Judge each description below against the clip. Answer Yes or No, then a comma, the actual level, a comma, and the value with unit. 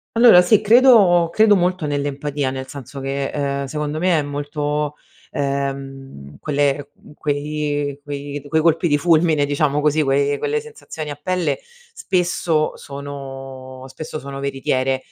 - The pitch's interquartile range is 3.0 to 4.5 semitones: No, narrow, 2.5 semitones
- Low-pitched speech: No, medium, 145 Hz